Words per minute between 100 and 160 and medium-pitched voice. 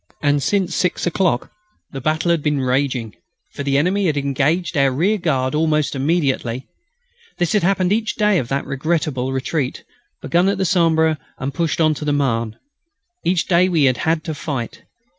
No: average, 170 wpm; medium, 155 Hz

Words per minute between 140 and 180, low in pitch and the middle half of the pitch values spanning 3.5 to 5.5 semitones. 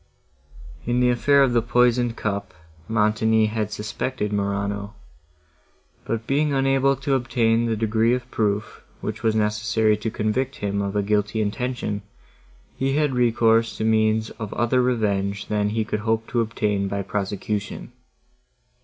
No: average, 145 wpm; low, 110 Hz; narrow, 2.6 semitones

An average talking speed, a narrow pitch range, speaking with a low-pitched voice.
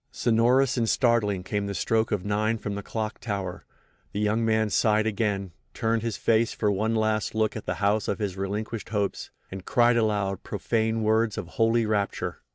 Yes: average, 180 wpm; narrow, 1.8 semitones; low, 110 Hz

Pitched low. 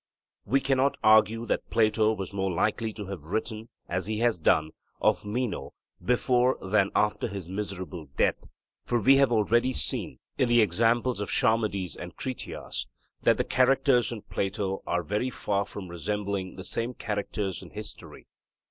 Yes: low, 105 Hz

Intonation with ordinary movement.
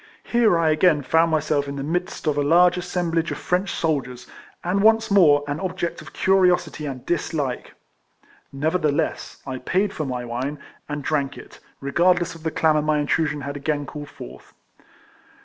Yes: average, 3.6 semitones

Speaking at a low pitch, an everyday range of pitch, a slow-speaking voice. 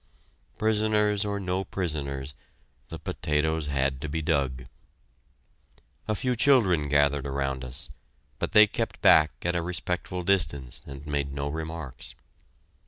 Yes: very low, 75 Hz; average, 4.8 semitones; slow, 130 wpm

